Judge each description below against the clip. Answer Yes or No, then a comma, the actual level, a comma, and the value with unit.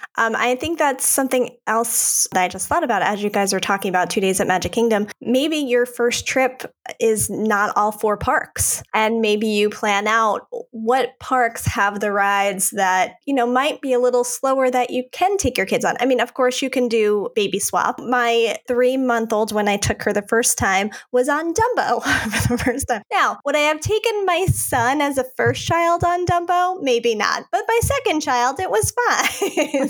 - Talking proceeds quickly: Yes, fast, 210 wpm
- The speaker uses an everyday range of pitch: Yes, average, 4.7 semitones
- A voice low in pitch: No, high, 245 Hz